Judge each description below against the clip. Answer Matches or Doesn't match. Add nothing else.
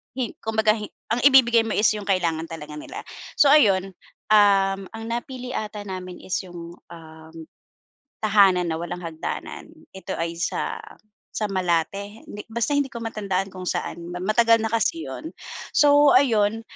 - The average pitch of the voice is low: Doesn't match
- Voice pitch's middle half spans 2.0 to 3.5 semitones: Doesn't match